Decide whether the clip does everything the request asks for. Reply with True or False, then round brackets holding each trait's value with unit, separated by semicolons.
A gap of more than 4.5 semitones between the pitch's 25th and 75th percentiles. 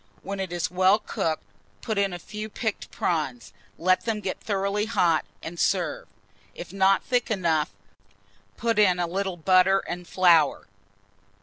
False (3.0 semitones)